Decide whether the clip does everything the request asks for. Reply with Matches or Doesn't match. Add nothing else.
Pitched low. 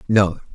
Matches